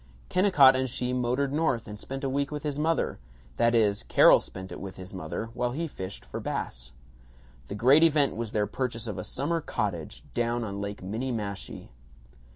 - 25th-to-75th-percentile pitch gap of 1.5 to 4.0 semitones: No, wide, 5.5 semitones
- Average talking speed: Yes, average, 185 wpm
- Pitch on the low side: Yes, low, 120 Hz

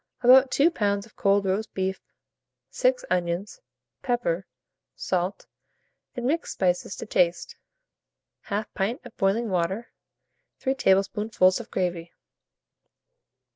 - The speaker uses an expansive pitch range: No, average, 4.3 semitones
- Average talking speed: No, slow, 110 wpm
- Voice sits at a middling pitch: No, high, 200 Hz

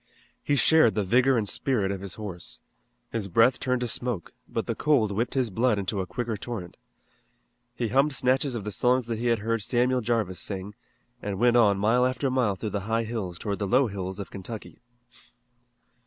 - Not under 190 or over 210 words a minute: Yes, average, 200 wpm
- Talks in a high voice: No, low, 115 Hz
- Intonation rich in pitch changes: No, average, 3.7 semitones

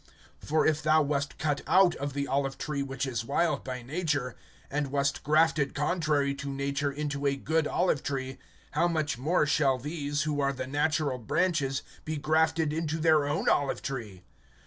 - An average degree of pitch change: No, narrow, 2.1 semitones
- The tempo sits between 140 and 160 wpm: No, average, 175 wpm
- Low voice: No, medium, 145 Hz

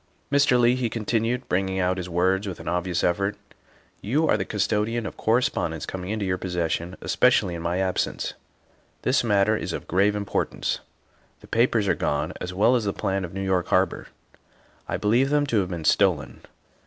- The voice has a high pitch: No, low, 100 Hz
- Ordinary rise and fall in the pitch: Yes, average, 3.9 semitones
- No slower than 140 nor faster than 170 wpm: No, average, 200 wpm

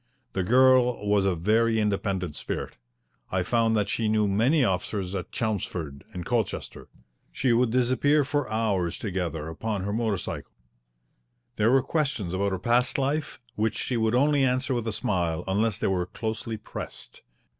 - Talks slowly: No, average, 165 wpm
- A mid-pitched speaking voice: No, low, 110 Hz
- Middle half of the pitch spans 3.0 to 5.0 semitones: Yes, average, 4.5 semitones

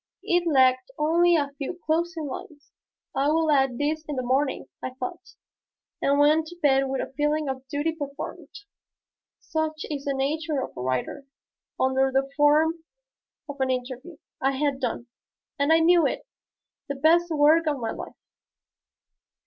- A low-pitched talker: No, very high, 290 Hz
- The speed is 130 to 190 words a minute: Yes, average, 160 wpm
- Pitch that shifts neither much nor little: Yes, average, 3.0 semitones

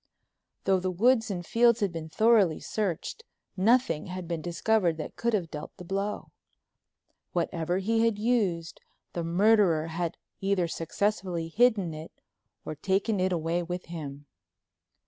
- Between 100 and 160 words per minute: Yes, average, 145 wpm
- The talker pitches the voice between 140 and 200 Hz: Yes, medium, 185 Hz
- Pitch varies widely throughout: No, average, 4.2 semitones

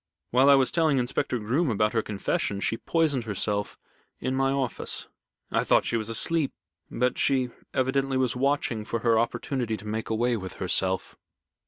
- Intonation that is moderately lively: Yes, average, 3.5 semitones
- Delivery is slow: No, average, 170 wpm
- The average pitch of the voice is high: No, low, 125 Hz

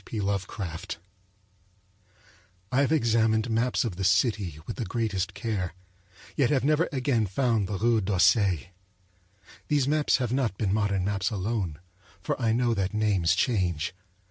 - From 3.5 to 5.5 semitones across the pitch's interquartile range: Yes, average, 3.8 semitones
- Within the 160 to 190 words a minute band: No, average, 145 wpm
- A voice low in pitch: Yes, low, 110 Hz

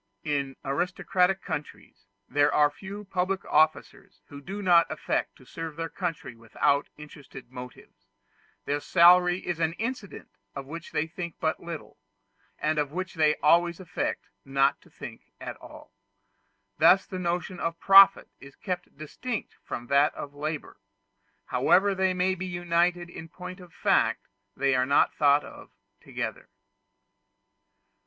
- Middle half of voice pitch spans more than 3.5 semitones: Yes, average, 3.9 semitones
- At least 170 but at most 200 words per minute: No, average, 145 wpm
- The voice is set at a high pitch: No, medium, 165 Hz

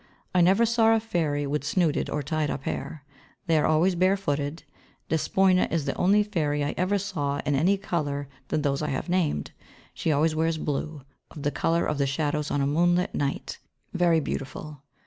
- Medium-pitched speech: Yes, medium, 155 Hz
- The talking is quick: No, average, 195 wpm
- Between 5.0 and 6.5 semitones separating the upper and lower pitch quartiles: No, average, 3.9 semitones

